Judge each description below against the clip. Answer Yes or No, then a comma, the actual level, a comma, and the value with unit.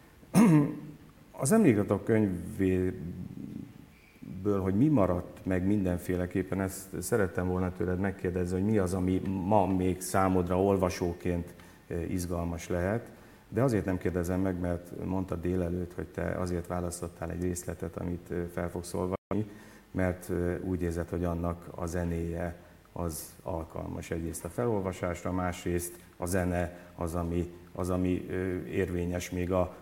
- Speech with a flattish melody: Yes, narrow, 1.5 semitones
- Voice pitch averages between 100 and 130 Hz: No, very low, 90 Hz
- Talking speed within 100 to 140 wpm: Yes, average, 130 wpm